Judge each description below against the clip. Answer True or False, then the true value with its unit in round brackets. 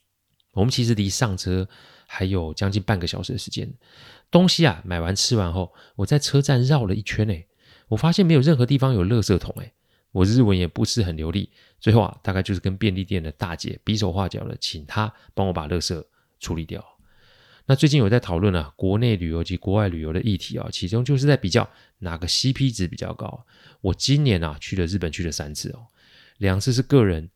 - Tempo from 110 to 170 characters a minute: False (310 characters per minute)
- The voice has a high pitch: False (105 Hz)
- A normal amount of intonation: True (4.9 semitones)